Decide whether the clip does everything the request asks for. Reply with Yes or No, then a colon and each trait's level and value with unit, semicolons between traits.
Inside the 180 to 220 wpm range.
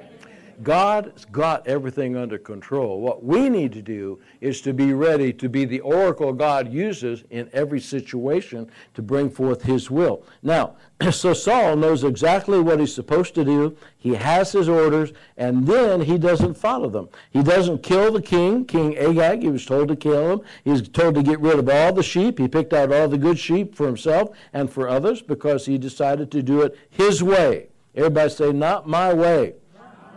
Yes: average, 190 wpm